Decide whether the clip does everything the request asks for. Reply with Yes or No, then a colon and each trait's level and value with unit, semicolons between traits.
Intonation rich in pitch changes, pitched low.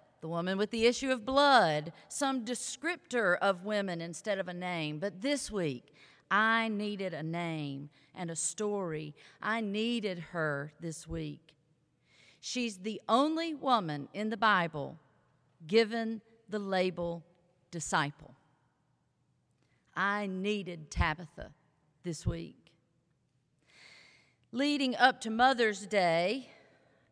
No: wide, 6.2 semitones; medium, 185 Hz